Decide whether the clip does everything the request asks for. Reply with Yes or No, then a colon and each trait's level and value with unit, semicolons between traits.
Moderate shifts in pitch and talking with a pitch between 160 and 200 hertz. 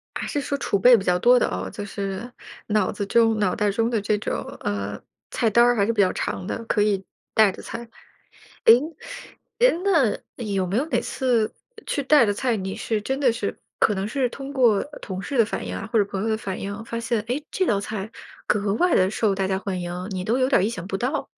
No: average, 3.7 semitones; high, 215 Hz